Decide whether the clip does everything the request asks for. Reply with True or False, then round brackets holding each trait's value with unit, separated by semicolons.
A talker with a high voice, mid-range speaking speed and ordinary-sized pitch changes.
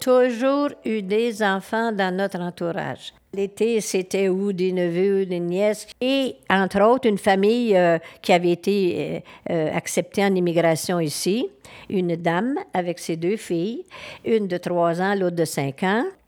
True (195 Hz; 160 wpm; 3.8 semitones)